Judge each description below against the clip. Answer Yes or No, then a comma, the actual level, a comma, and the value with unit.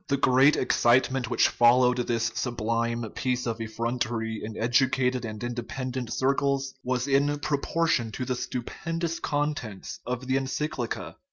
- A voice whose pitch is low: Yes, low, 125 Hz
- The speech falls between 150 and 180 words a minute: No, average, 140 wpm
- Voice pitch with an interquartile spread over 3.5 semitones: No, narrow, 2.4 semitones